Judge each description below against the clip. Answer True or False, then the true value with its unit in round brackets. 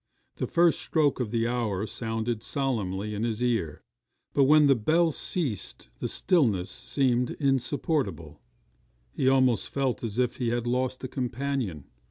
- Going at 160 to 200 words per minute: False (150 wpm)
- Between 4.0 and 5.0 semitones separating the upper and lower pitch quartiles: False (3.6 semitones)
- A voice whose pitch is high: False (125 Hz)